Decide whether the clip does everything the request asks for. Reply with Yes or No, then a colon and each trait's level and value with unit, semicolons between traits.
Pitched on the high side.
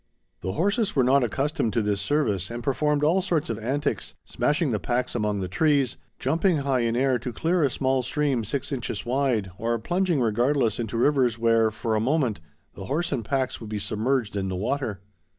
No: low, 125 Hz